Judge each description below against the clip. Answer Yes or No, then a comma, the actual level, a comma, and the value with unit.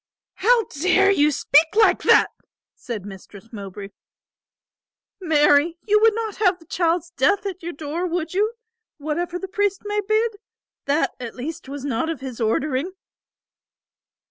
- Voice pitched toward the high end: Yes, very high, 330 Hz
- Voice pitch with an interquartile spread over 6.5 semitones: No, wide, 5.8 semitones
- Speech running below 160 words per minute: Yes, average, 145 wpm